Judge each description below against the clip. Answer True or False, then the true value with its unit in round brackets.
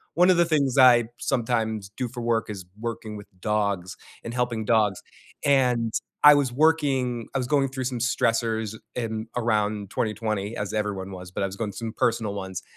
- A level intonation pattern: False (3.1 semitones)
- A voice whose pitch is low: True (115 Hz)